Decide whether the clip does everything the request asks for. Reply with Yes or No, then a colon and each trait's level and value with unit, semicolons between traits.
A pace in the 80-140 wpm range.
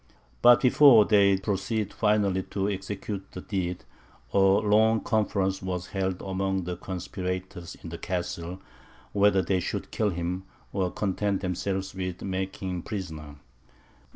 Yes: slow, 135 wpm